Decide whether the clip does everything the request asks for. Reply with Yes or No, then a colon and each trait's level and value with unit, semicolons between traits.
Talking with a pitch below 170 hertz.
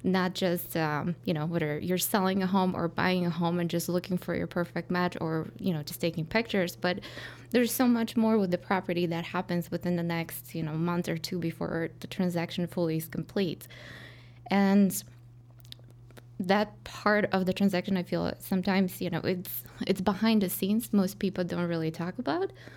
No: medium, 175 Hz